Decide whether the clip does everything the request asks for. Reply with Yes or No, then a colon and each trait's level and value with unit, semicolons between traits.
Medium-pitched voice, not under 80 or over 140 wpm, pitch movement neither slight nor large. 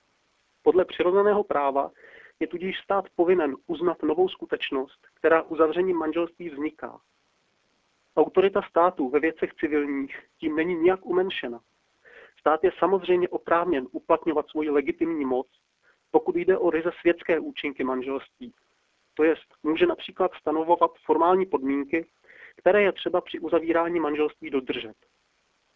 Yes: medium, 170 Hz; average, 120 wpm; average, 3.5 semitones